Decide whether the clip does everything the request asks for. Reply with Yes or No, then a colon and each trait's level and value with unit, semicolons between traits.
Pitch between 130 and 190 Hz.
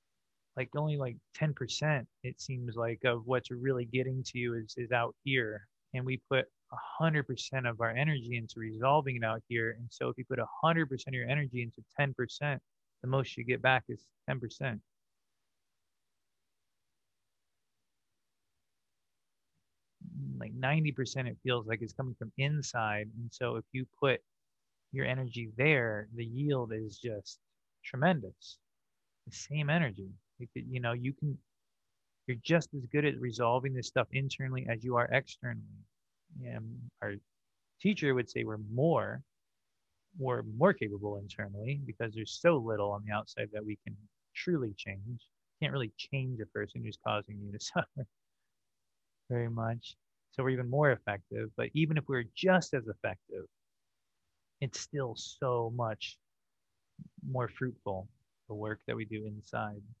No: low, 120 Hz